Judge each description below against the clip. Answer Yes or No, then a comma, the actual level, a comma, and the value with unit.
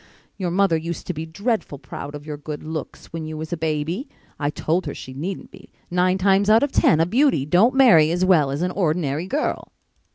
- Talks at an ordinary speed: No, fast, 220 wpm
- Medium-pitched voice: Yes, medium, 165 Hz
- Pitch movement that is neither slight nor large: Yes, average, 3.9 semitones